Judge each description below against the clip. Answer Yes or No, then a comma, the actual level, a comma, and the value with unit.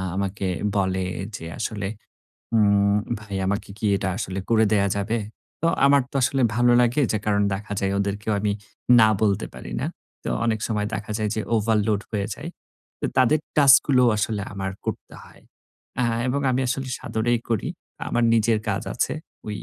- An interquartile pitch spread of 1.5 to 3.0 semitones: Yes, average, 2.7 semitones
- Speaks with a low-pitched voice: Yes, low, 110 Hz